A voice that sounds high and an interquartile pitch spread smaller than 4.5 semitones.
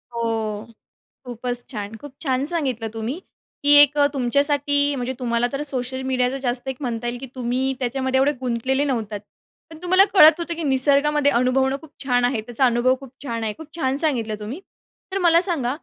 Yes: very high, 260 Hz; average, 3.1 semitones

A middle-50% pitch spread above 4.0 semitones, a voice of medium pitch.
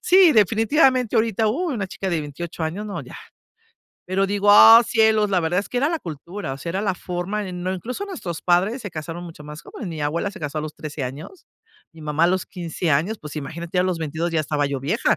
Yes: average, 5.0 semitones; medium, 180 Hz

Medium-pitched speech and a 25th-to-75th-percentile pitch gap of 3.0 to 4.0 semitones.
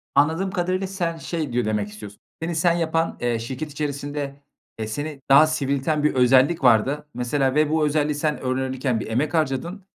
Yes: medium, 145 Hz; average, 3.6 semitones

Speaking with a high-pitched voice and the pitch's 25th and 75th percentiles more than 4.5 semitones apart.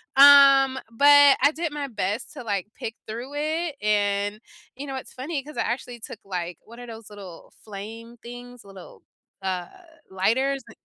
Yes: high, 235 Hz; average, 5.1 semitones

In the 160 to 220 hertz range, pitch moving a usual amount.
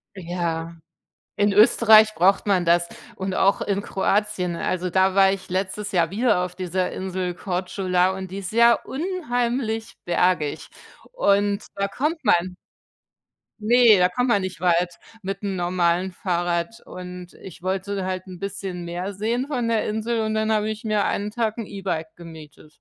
Yes: high, 190 Hz; average, 3.1 semitones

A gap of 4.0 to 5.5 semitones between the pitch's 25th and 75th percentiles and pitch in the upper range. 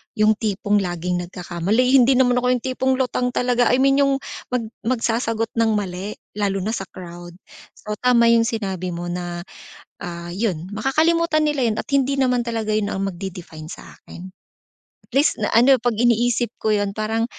Yes: average, 4.8 semitones; high, 220 Hz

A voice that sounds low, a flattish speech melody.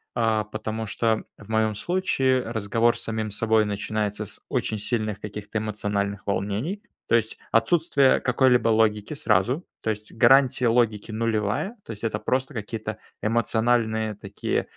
Yes: low, 110 Hz; narrow, 2.1 semitones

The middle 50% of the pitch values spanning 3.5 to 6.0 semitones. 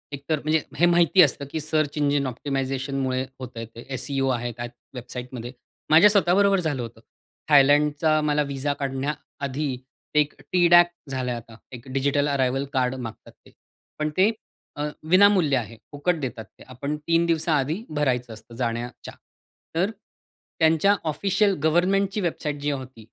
Yes: average, 3.9 semitones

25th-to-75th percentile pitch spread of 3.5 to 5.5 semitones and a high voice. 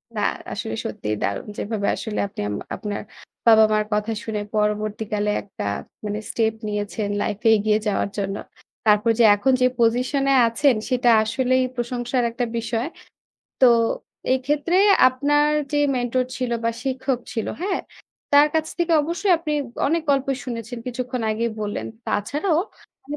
Yes: average, 4.2 semitones; high, 240 Hz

